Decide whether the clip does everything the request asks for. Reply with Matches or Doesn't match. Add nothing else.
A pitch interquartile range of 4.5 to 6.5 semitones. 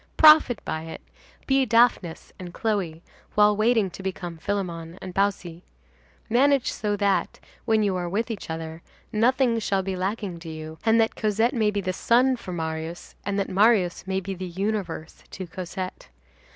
Doesn't match